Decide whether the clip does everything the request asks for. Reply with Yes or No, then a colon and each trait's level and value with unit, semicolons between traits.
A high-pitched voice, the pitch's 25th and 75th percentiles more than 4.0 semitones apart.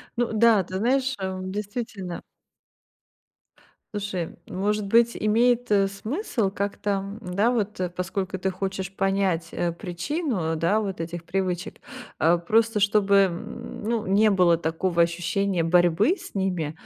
No: high, 195 Hz; average, 3.2 semitones